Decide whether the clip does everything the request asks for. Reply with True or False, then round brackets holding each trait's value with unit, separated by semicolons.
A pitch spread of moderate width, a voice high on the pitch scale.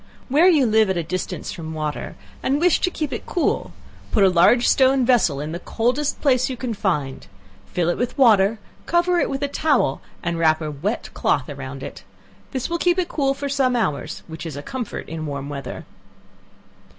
False (9.0 semitones; 225 Hz)